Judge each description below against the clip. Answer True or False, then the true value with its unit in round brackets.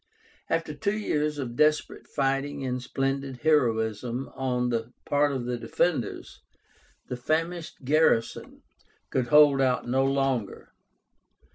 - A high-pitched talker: False (135 Hz)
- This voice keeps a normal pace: False (120 wpm)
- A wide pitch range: False (3.3 semitones)